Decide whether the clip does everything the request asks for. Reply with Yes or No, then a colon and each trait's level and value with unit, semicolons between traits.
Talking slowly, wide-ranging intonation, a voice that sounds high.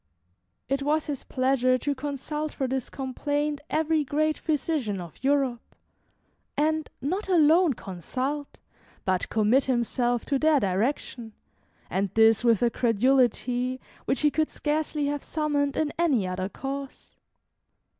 No: slow, 130 wpm; average, 3.7 semitones; very high, 275 Hz